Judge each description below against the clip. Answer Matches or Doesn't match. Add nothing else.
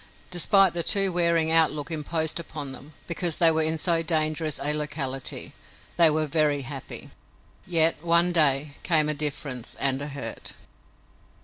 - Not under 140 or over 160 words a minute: Matches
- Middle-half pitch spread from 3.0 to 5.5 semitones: Doesn't match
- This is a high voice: Doesn't match